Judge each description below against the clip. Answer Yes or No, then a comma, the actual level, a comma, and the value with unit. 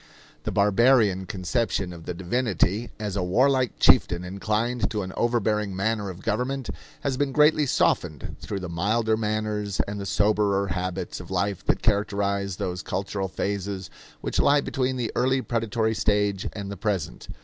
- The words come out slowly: No, average, 160 wpm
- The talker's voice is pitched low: Yes, low, 105 Hz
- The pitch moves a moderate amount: Yes, average, 3.4 semitones